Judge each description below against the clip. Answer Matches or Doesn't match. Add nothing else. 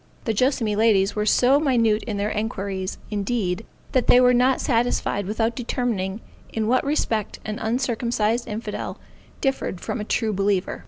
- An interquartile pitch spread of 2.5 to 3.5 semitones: Matches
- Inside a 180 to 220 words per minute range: Doesn't match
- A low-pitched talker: Doesn't match